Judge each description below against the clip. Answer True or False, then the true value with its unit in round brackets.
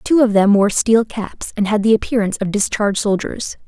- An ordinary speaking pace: False (210 wpm)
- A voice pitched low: False (210 Hz)